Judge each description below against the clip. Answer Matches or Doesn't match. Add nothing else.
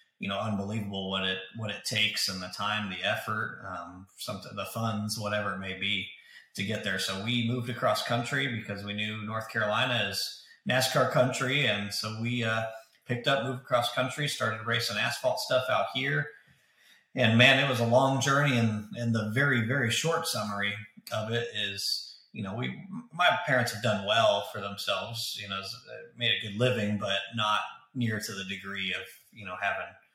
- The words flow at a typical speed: Matches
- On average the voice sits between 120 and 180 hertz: Doesn't match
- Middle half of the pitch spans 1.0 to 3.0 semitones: Doesn't match